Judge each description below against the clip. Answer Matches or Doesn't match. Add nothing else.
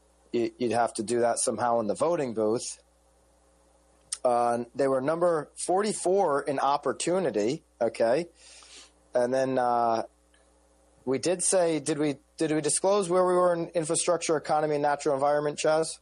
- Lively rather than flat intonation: Matches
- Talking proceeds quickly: Doesn't match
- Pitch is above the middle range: Doesn't match